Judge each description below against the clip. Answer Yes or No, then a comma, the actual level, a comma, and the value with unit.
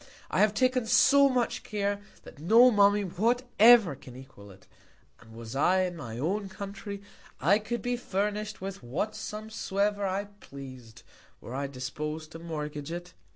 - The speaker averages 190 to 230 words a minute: No, average, 160 wpm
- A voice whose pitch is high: Yes, high, 195 Hz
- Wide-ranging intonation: Yes, wide, 6.7 semitones